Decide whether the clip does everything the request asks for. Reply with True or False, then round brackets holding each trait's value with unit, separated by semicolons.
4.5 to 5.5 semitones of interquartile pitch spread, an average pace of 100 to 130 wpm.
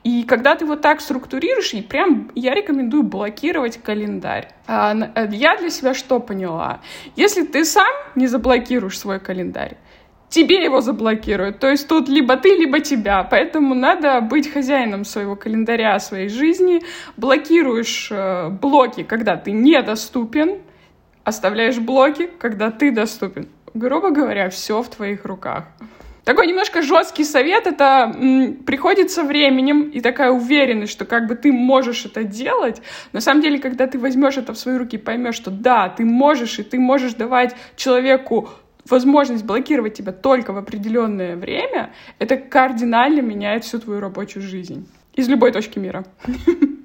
False (4.8 semitones; 145 wpm)